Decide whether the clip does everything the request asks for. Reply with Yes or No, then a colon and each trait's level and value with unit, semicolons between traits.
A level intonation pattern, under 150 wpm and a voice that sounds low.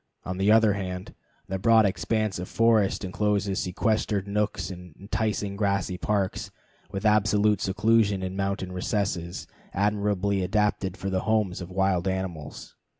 Yes: narrow, 2.0 semitones; average, 140 wpm; low, 100 Hz